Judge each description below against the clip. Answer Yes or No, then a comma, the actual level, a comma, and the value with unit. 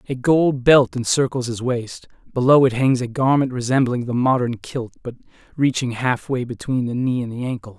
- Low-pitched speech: Yes, low, 125 Hz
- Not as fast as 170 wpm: No, average, 185 wpm